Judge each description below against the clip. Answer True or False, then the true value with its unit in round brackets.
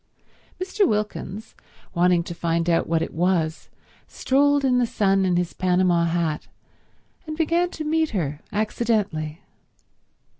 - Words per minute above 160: False (135 wpm)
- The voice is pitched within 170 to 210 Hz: True (185 Hz)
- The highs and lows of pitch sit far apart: True (7.0 semitones)